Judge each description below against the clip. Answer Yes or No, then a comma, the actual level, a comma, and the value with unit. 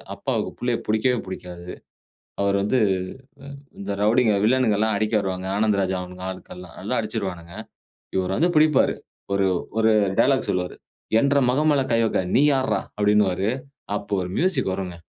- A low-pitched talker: Yes, low, 105 Hz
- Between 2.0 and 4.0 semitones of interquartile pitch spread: No, average, 4.7 semitones